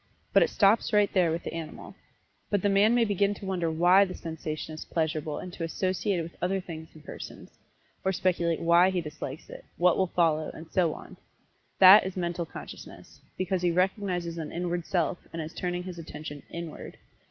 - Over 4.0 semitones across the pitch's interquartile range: No, narrow, 2.5 semitones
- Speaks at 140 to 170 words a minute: No, average, 200 wpm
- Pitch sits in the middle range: Yes, medium, 175 Hz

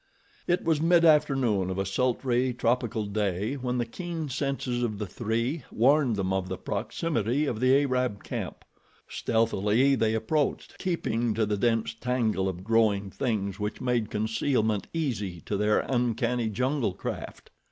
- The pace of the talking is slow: No, average, 150 wpm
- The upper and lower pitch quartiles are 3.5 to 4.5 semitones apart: Yes, average, 4.0 semitones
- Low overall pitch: Yes, low, 115 Hz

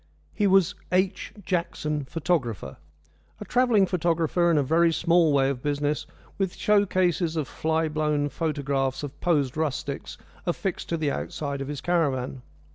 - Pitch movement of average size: Yes, average, 3.5 semitones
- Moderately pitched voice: Yes, medium, 160 Hz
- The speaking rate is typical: Yes, average, 150 wpm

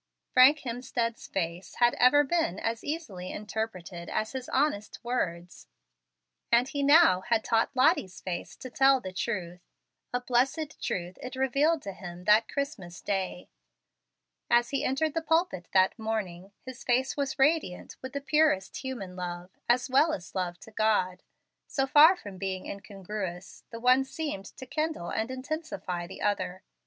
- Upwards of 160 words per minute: No, average, 155 wpm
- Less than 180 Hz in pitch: No, high, 230 Hz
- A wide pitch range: Yes, wide, 6.3 semitones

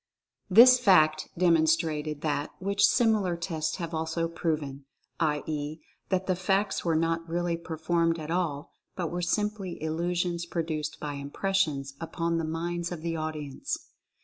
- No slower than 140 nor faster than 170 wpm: Yes, average, 145 wpm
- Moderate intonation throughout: No, narrow, 2.2 semitones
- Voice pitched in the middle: Yes, medium, 165 Hz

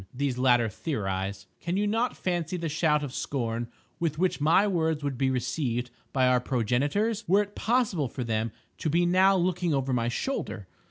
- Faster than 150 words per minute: Yes, average, 180 wpm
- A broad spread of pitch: Yes, wide, 6.5 semitones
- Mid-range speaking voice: Yes, medium, 145 Hz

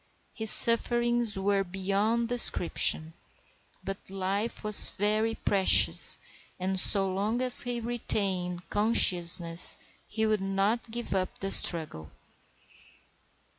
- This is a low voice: No, high, 200 Hz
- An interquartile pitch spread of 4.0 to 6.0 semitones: No, average, 3.2 semitones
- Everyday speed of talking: No, slow, 105 wpm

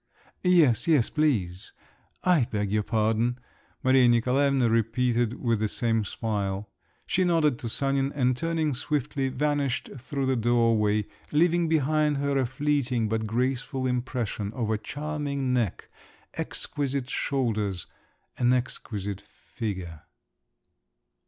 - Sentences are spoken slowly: Yes, slow, 120 wpm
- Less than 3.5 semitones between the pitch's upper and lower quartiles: No, average, 4.1 semitones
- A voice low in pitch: Yes, low, 125 Hz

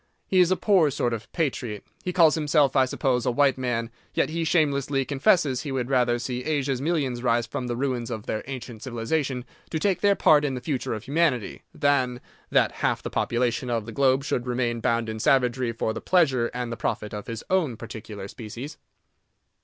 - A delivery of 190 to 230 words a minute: Yes, average, 200 wpm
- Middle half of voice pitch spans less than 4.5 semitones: Yes, average, 3.6 semitones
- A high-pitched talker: No, low, 130 Hz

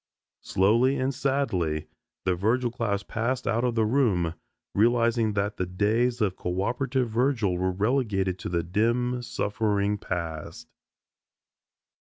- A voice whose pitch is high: No, low, 110 Hz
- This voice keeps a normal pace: No, slow, 125 wpm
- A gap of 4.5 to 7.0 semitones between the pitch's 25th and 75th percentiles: Yes, average, 4.8 semitones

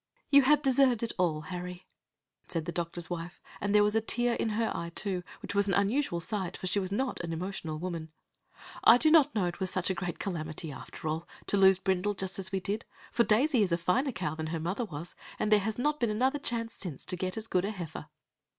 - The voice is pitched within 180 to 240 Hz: Yes, high, 190 Hz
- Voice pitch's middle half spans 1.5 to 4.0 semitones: No, average, 4.4 semitones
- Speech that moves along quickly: Yes, fast, 240 wpm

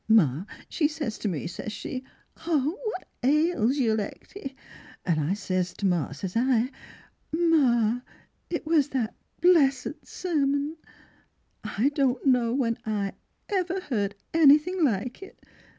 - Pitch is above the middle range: Yes, very high, 260 Hz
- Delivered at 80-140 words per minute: Yes, slow, 135 wpm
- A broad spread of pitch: Yes, wide, 6.4 semitones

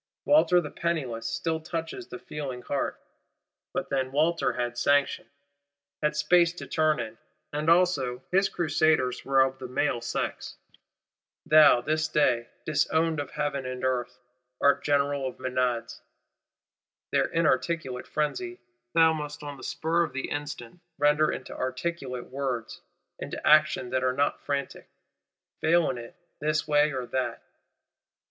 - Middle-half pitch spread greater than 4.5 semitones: No, average, 3.6 semitones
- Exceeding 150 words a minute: No, average, 140 wpm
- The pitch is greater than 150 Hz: No, medium, 145 Hz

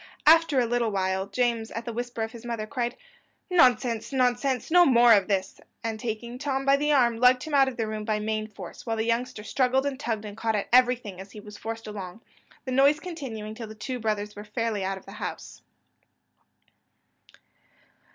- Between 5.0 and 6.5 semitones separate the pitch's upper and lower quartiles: No, average, 2.9 semitones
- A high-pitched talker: Yes, high, 230 Hz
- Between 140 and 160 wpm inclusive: No, average, 200 wpm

